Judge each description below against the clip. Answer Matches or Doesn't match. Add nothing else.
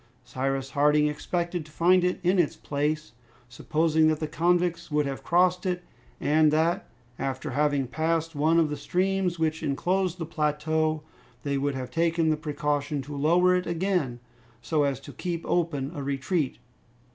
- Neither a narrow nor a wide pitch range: Matches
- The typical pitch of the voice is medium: Matches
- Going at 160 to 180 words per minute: Matches